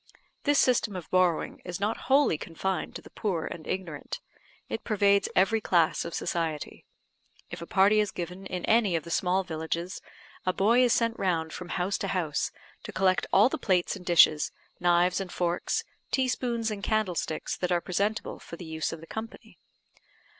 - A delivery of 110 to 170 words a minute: No, average, 180 wpm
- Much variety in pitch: No, average, 3.7 semitones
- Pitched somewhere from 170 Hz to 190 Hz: Yes, medium, 185 Hz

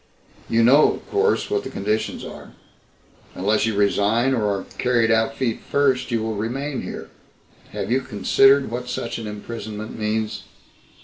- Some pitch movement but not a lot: Yes, average, 3.3 semitones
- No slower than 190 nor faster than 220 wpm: No, average, 160 wpm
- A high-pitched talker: No, low, 115 Hz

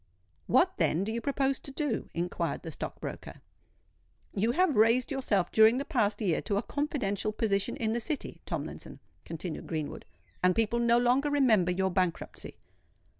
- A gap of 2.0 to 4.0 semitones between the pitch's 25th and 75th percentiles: No, wide, 5.5 semitones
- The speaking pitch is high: Yes, high, 225 Hz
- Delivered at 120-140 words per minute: No, average, 165 wpm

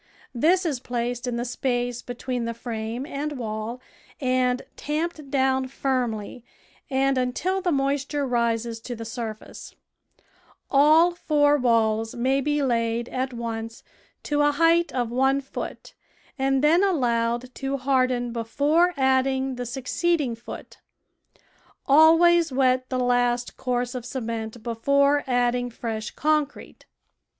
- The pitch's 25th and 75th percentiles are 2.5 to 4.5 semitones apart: Yes, average, 3.0 semitones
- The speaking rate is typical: No, slow, 125 wpm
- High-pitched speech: Yes, very high, 255 Hz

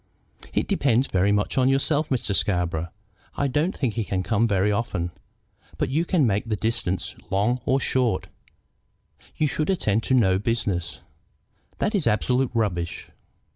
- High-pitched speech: No, low, 115 Hz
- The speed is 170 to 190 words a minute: No, average, 155 wpm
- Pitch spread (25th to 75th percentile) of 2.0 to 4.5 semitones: No, wide, 5.6 semitones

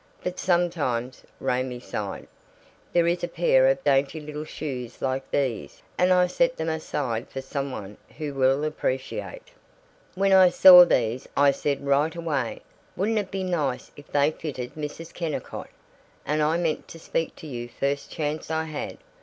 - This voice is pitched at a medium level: Yes, medium, 150 Hz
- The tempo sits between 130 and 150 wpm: No, average, 165 wpm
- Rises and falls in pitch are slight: No, average, 4.1 semitones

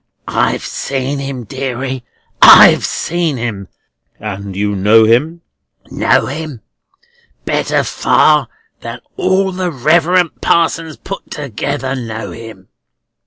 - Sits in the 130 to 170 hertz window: Yes, low, 135 Hz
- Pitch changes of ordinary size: No, wide, 6.3 semitones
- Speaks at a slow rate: Yes, slow, 110 wpm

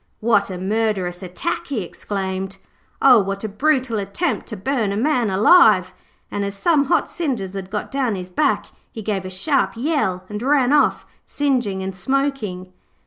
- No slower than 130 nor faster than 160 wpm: No, average, 170 wpm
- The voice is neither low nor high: No, high, 210 Hz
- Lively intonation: Yes, wide, 6.0 semitones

